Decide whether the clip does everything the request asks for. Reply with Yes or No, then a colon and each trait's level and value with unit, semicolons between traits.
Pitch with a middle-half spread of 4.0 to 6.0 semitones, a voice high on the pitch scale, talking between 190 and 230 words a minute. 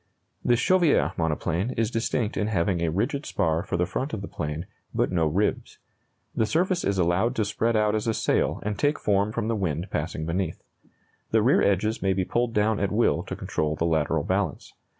No: average, 5.2 semitones; low, 100 Hz; fast, 205 wpm